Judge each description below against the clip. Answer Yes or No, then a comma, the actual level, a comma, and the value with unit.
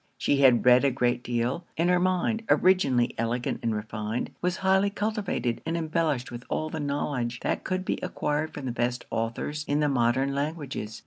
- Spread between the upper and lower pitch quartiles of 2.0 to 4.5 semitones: No, wide, 5.6 semitones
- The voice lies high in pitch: No, medium, 140 Hz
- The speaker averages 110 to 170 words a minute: No, average, 185 wpm